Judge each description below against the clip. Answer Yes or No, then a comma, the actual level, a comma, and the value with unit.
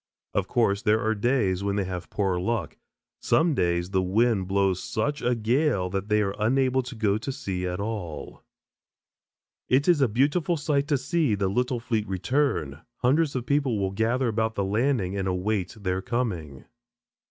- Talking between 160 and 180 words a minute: Yes, average, 175 wpm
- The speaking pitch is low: Yes, low, 110 Hz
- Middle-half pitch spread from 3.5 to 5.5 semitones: Yes, average, 5.1 semitones